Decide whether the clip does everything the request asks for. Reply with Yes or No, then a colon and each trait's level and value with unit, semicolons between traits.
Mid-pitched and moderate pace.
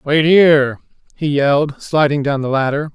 Yes: medium, 145 Hz; average, 165 wpm